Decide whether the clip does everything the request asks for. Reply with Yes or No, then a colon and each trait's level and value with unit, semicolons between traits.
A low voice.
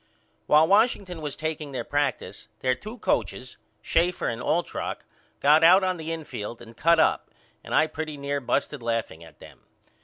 No: medium, 150 Hz